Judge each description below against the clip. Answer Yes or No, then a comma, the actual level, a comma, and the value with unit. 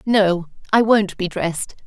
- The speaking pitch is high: Yes, high, 195 Hz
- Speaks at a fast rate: No, average, 160 wpm